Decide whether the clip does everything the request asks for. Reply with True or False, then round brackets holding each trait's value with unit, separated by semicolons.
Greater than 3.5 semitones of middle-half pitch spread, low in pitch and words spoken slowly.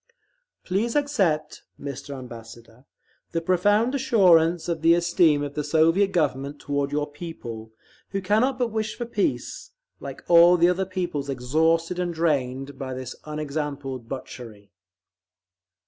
False (4.7 semitones; 160 Hz; 130 wpm)